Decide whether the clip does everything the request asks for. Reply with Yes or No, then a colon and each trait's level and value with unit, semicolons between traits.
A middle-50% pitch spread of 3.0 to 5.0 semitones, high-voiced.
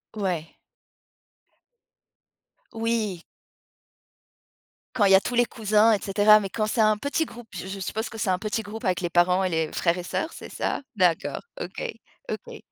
Yes: average, 3.4 semitones; high, 205 Hz